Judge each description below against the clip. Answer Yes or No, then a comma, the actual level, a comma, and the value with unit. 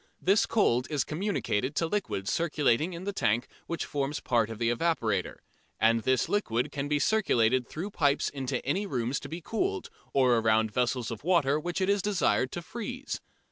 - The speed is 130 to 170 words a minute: No, average, 185 wpm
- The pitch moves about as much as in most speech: No, wide, 7.2 semitones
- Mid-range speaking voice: Yes, medium, 145 Hz